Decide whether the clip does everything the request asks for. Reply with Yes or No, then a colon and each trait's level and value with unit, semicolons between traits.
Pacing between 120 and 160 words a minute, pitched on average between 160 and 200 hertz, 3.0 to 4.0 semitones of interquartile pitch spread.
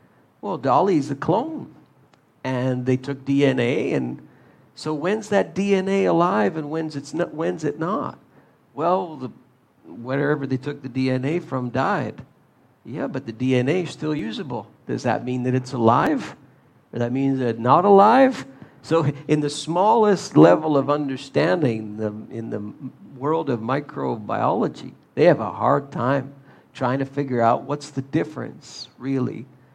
No: average, 155 wpm; low, 135 Hz; average, 3.3 semitones